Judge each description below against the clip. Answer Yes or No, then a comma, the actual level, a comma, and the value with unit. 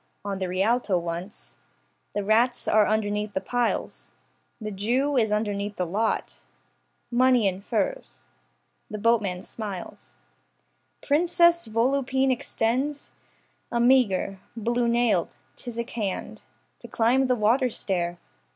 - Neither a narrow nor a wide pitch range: Yes, average, 3.7 semitones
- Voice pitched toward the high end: Yes, high, 225 Hz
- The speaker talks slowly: Yes, slow, 115 wpm